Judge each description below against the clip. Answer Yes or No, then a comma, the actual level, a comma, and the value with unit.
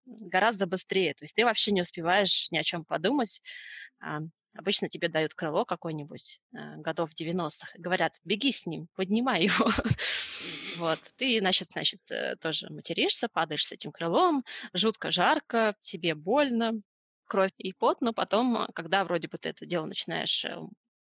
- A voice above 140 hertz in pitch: Yes, high, 190 Hz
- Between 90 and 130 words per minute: No, average, 150 wpm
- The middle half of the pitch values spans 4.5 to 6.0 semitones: Yes, average, 5.0 semitones